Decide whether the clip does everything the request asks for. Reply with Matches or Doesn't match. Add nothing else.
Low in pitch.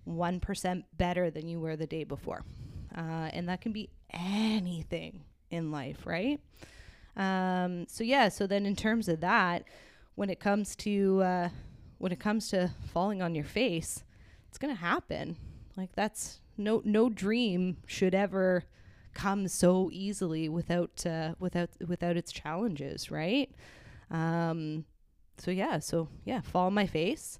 Doesn't match